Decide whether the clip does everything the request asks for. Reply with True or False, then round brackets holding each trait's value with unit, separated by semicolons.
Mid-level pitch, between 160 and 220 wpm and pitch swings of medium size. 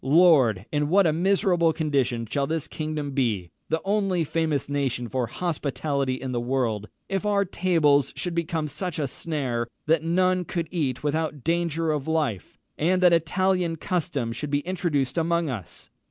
True (155 Hz; 170 wpm; 4.1 semitones)